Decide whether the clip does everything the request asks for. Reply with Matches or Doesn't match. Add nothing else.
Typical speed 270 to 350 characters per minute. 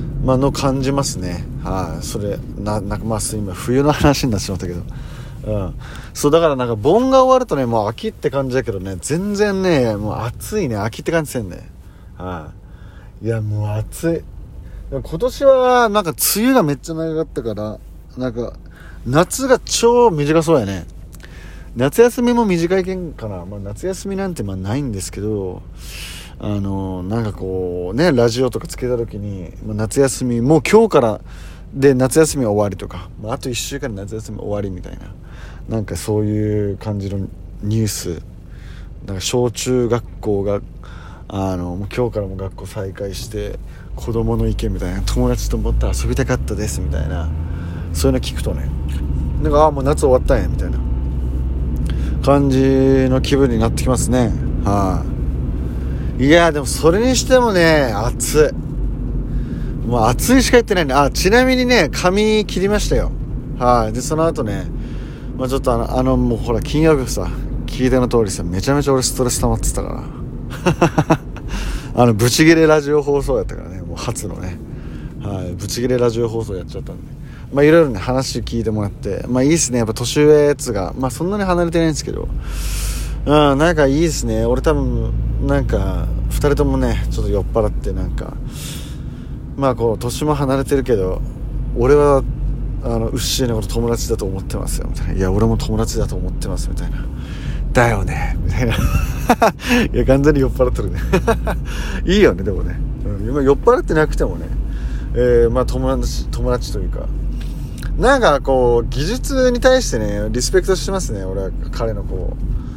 Matches